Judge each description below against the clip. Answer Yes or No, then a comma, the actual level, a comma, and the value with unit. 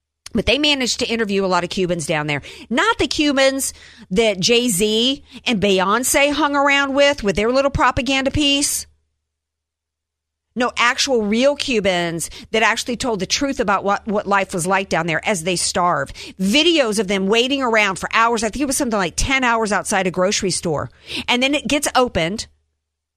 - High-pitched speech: Yes, high, 220 Hz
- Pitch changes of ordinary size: No, wide, 6.3 semitones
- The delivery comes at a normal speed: Yes, average, 180 wpm